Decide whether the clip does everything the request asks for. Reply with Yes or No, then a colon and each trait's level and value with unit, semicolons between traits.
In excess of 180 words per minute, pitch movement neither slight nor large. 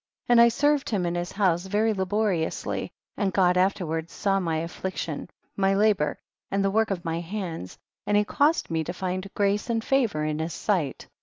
Yes: average, 190 wpm; average, 3.6 semitones